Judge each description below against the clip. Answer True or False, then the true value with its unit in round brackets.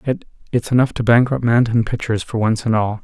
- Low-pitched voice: True (115 Hz)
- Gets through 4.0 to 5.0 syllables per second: False (6.1 syllables/s)